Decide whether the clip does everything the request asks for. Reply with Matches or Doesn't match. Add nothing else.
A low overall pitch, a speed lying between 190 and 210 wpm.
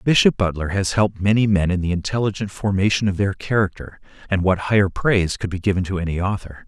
Matches